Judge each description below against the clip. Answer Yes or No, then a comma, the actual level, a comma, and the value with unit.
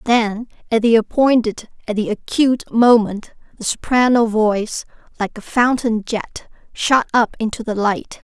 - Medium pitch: No, high, 225 Hz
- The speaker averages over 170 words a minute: No, average, 145 wpm